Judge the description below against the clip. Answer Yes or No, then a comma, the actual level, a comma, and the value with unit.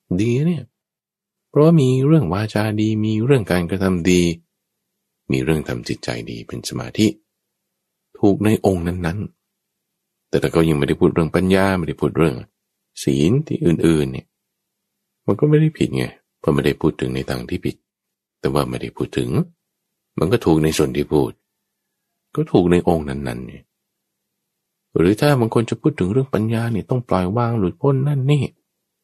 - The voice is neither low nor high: No, low, 105 Hz